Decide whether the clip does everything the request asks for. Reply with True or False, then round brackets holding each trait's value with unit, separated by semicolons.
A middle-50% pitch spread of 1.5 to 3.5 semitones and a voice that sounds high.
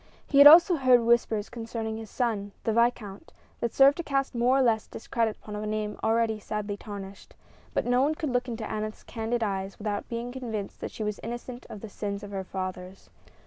True (2.9 semitones; 225 Hz)